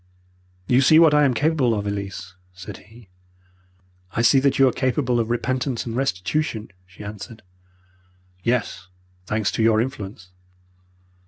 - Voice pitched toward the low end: Yes, low, 115 Hz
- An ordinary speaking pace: Yes, average, 145 wpm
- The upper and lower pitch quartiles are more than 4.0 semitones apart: Yes, average, 4.4 semitones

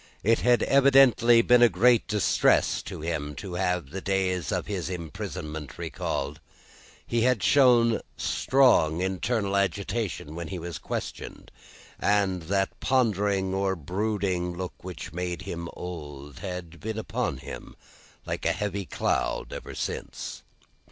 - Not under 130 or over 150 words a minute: Yes, slow, 135 wpm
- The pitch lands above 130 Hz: No, very low, 95 Hz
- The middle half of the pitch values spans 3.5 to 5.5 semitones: Yes, average, 4.3 semitones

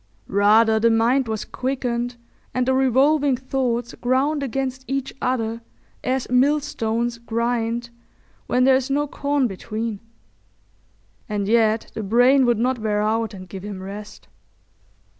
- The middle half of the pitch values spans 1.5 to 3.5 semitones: Yes, average, 2.9 semitones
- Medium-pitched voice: No, high, 240 Hz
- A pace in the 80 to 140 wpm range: Yes, slow, 135 wpm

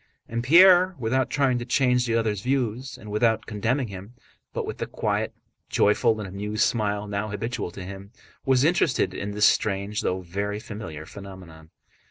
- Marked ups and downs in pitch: No, average, 3.8 semitones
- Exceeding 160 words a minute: Yes, average, 170 wpm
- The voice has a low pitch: Yes, low, 110 Hz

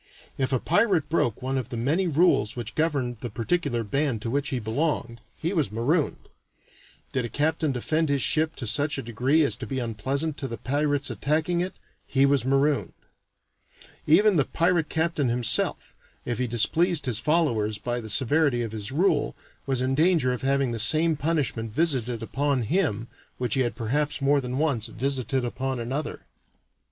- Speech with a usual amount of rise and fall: Yes, average, 4.4 semitones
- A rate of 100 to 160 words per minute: No, average, 180 wpm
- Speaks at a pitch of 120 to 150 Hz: Yes, low, 135 Hz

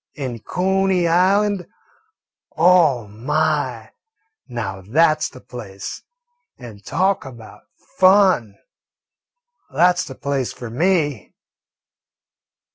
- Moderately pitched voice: Yes, medium, 150 Hz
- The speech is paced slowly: Yes, slow, 95 wpm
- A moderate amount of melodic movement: No, wide, 7.4 semitones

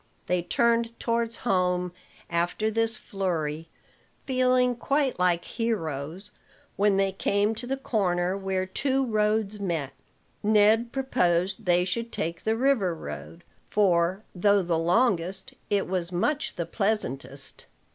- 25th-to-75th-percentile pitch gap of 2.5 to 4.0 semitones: No, average, 4.6 semitones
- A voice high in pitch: Yes, high, 195 Hz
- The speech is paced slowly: Yes, slow, 125 wpm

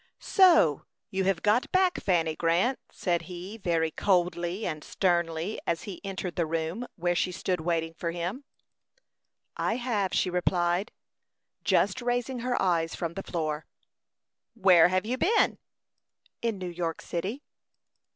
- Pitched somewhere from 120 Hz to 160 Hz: No, medium, 180 Hz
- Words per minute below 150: Yes, average, 140 wpm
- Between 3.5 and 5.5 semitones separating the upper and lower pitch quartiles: Yes, average, 4.0 semitones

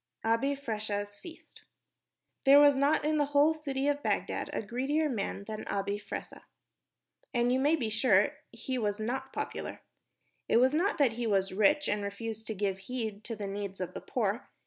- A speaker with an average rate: Yes, average, 185 wpm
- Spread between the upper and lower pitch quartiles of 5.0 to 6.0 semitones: Yes, wide, 5.4 semitones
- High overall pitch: Yes, high, 230 Hz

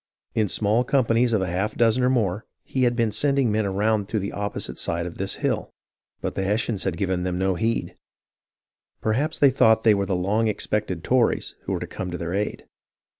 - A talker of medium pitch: No, low, 105 Hz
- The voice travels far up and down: No, average, 3.3 semitones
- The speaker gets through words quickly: Yes, fast, 210 wpm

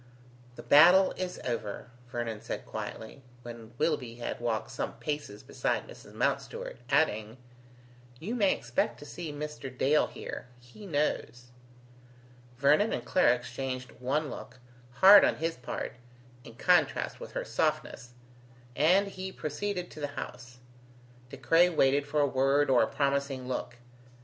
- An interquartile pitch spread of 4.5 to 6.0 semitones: Yes, average, 5.0 semitones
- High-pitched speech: No, medium, 140 Hz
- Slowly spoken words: No, average, 145 wpm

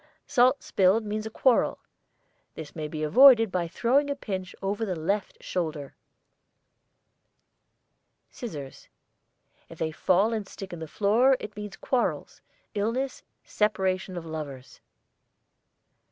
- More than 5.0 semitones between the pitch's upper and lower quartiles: Yes, wide, 5.5 semitones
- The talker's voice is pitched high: Yes, high, 200 Hz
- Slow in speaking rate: Yes, slow, 125 wpm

